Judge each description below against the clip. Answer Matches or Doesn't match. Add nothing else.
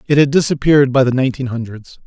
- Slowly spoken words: Doesn't match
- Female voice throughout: Doesn't match